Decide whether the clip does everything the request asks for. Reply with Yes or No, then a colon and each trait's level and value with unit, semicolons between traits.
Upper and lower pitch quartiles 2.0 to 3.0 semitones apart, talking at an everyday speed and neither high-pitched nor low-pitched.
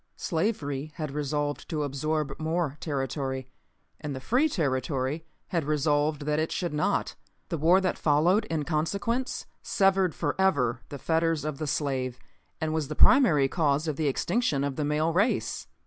Yes: average, 2.7 semitones; average, 160 wpm; medium, 155 Hz